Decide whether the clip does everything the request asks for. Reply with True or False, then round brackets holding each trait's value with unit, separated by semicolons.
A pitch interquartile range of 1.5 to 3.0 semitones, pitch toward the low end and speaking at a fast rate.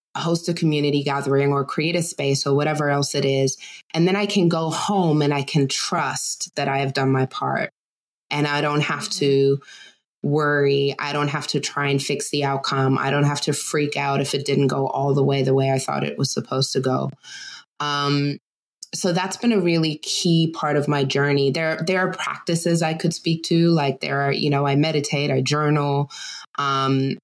False (2.5 semitones; 145 Hz; 210 wpm)